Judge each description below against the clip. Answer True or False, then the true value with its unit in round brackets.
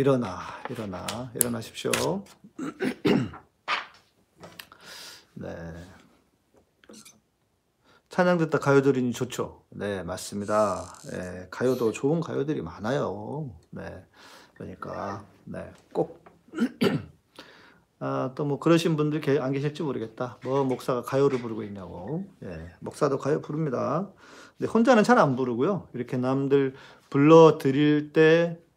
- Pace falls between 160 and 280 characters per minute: True (230 characters per minute)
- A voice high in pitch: False (130 Hz)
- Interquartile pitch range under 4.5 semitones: False (5.6 semitones)